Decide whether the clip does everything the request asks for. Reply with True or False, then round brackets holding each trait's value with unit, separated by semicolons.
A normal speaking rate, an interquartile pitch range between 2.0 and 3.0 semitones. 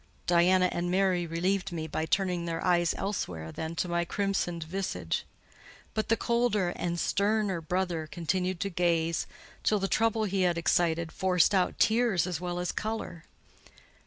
True (160 wpm; 2.6 semitones)